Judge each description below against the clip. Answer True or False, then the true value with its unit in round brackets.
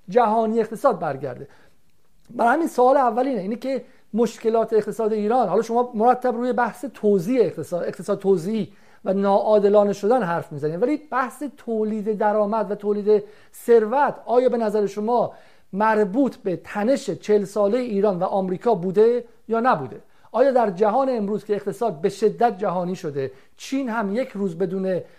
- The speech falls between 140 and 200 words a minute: True (150 wpm)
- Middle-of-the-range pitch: False (220 Hz)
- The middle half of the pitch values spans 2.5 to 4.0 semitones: True (3.3 semitones)